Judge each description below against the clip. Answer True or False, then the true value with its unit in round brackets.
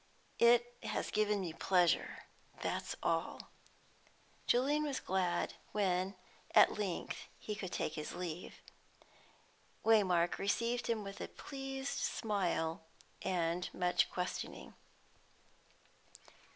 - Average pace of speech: False (100 wpm)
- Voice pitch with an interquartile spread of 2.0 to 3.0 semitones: False (4.7 semitones)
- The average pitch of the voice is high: True (195 Hz)